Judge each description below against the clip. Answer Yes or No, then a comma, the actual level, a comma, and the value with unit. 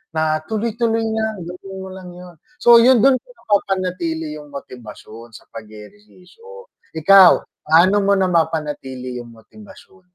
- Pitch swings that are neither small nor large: No, wide, 5.9 semitones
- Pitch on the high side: No, medium, 180 Hz